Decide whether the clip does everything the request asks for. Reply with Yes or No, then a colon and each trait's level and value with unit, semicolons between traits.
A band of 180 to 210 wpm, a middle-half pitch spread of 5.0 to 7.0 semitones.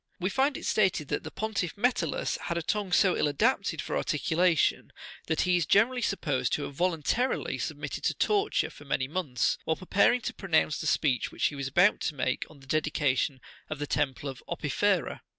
Yes: average, 200 wpm; wide, 5.5 semitones